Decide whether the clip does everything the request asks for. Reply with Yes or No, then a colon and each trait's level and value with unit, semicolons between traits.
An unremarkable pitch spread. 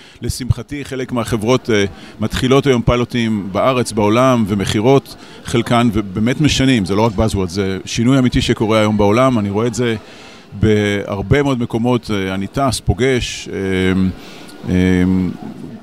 Yes: average, 3.6 semitones